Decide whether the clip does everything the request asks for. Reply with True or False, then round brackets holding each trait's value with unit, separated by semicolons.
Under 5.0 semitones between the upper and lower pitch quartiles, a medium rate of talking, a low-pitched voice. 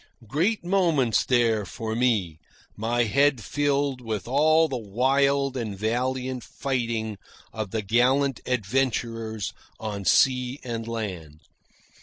False (3.7 semitones; 115 wpm; 120 Hz)